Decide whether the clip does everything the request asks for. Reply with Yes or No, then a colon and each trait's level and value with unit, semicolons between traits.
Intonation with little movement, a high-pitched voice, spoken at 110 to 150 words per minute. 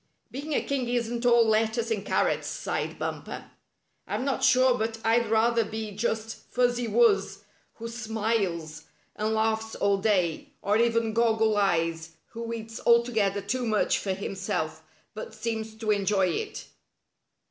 Yes: narrow, 2.3 semitones; high, 220 Hz; average, 145 wpm